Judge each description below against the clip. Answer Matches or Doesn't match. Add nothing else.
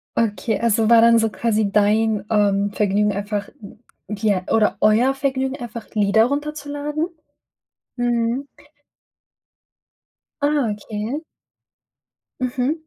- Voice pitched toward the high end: Matches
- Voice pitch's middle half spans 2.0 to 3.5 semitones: Doesn't match